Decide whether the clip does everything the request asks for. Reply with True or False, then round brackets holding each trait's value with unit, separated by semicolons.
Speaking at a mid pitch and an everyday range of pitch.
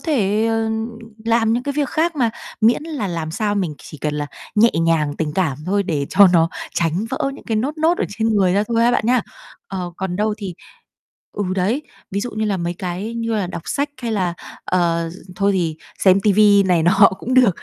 False (200 Hz; 4.5 semitones)